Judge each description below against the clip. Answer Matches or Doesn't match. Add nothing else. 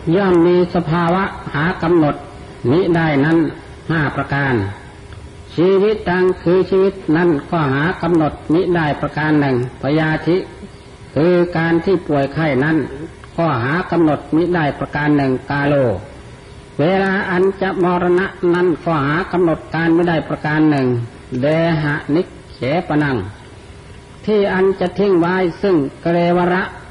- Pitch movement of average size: Matches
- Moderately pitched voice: Matches